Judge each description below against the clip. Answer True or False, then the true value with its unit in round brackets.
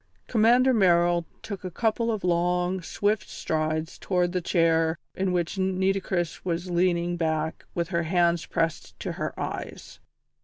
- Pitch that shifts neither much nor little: False (2.0 semitones)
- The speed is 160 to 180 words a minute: False (145 wpm)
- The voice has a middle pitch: True (175 Hz)